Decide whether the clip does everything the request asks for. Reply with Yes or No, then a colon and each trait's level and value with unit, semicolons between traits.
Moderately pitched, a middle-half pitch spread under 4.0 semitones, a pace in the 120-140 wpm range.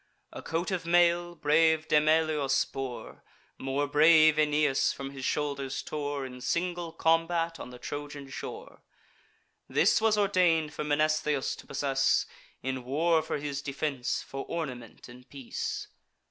Yes: medium, 150 Hz; average, 3.3 semitones; slow, 135 wpm